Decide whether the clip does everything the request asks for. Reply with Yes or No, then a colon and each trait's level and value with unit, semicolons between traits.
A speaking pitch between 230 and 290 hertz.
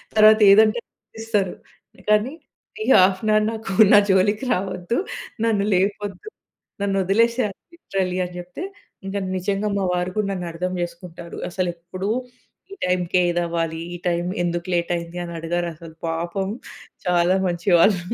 No: medium, 185 Hz